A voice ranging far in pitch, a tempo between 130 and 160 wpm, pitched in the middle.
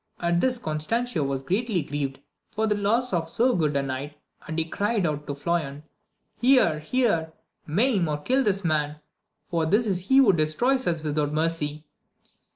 No: wide, 6.4 semitones; average, 170 wpm; medium, 165 Hz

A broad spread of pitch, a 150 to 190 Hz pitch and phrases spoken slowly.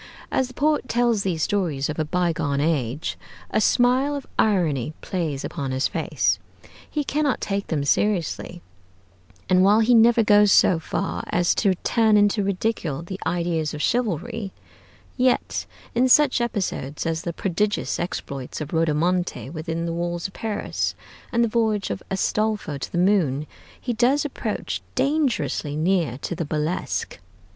No: wide, 5.9 semitones; medium, 185 Hz; average, 150 wpm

